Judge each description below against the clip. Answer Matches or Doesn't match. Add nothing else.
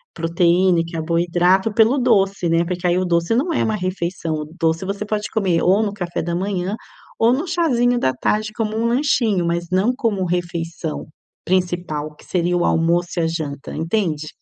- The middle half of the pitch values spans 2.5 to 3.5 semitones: Doesn't match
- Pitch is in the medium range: Matches